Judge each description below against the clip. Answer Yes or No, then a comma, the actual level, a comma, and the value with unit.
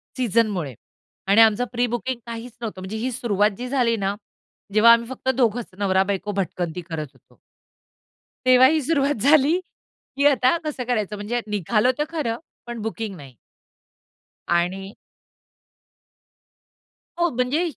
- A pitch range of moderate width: Yes, average, 4.2 semitones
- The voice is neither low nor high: No, high, 230 Hz